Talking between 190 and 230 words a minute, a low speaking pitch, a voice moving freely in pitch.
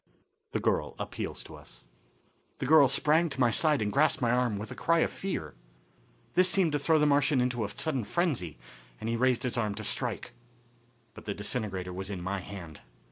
Yes: average, 200 wpm; low, 125 Hz; wide, 6.8 semitones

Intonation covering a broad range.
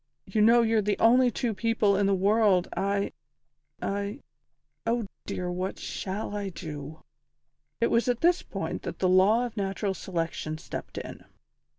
No: average, 3.3 semitones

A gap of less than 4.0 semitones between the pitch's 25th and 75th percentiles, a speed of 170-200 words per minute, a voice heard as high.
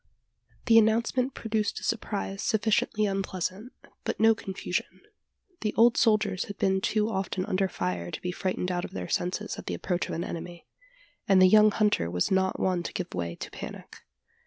Yes: average, 2.9 semitones; average, 185 wpm; high, 195 Hz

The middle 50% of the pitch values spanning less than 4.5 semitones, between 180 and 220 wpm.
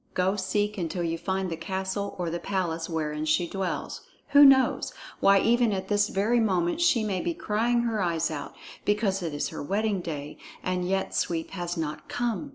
Yes: average, 3.7 semitones; average, 190 wpm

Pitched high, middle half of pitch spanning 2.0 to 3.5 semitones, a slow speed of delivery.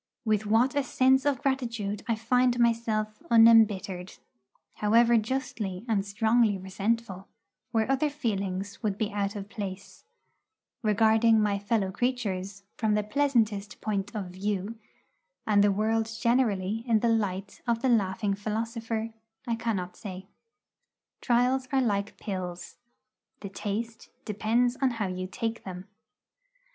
Yes: high, 215 Hz; average, 2.7 semitones; slow, 130 wpm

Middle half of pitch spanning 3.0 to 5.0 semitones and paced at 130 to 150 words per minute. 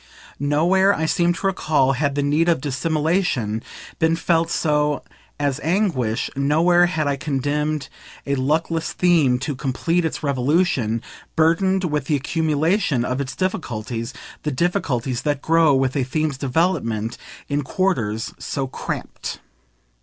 Yes: average, 3.9 semitones; slow, 135 wpm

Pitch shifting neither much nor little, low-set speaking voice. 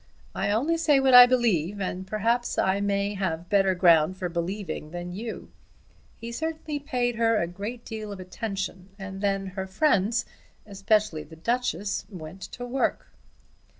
No: average, 4.1 semitones; high, 200 Hz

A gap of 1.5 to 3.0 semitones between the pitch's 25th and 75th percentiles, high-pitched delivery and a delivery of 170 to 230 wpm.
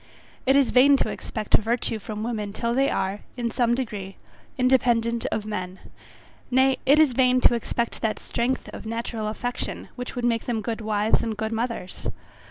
Yes: narrow, 2.5 semitones; high, 235 Hz; average, 180 wpm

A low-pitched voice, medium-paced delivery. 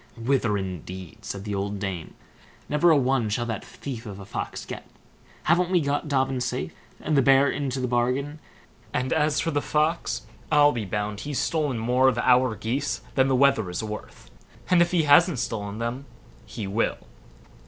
Yes: low, 125 Hz; average, 185 wpm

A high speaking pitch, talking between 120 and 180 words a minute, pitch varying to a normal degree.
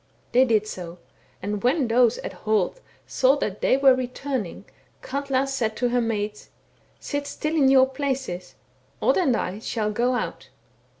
Yes: very high, 250 Hz; average, 170 wpm; average, 4.0 semitones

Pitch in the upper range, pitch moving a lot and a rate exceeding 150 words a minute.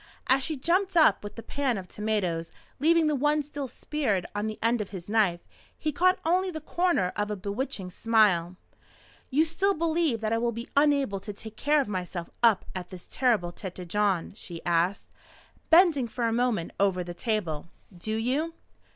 Yes: high, 225 Hz; wide, 7.6 semitones; average, 185 wpm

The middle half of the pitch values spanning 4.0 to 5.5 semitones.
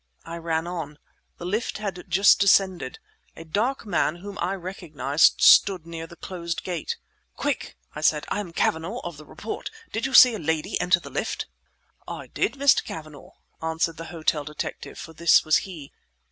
No: average, 3.4 semitones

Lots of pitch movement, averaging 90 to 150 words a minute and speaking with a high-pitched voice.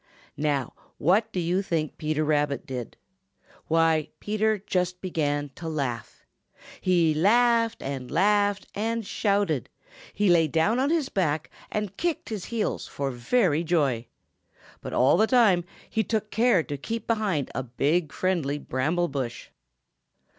No: wide, 6.2 semitones; average, 140 wpm; medium, 175 Hz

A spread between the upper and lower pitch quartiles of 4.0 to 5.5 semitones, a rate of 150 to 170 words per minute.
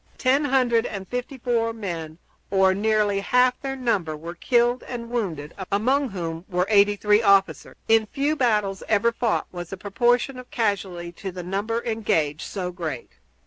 Yes: average, 4.7 semitones; average, 160 wpm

